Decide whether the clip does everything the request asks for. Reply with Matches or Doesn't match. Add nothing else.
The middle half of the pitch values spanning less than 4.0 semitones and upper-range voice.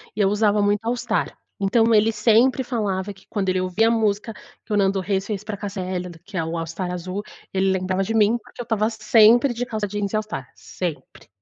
Matches